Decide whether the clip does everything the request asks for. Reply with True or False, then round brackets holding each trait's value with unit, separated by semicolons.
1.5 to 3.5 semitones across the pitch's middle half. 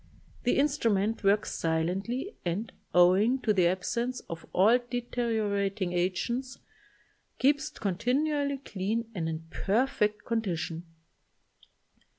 False (4.9 semitones)